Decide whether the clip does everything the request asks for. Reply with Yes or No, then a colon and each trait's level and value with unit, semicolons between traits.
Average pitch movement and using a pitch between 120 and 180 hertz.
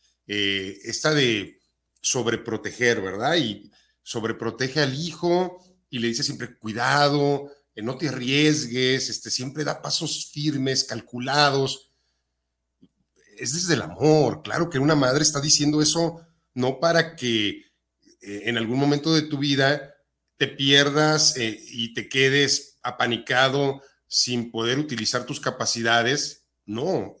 Yes: average, 4.2 semitones; low, 135 Hz